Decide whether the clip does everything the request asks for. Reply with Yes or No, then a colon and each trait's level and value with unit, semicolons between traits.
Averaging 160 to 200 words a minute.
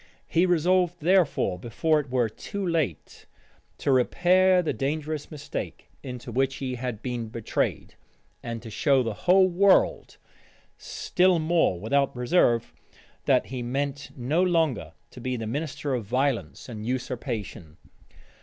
No: slow, 135 wpm